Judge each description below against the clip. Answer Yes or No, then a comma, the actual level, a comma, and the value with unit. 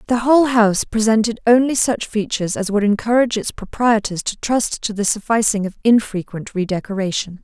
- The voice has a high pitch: Yes, high, 215 Hz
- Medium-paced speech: Yes, average, 170 wpm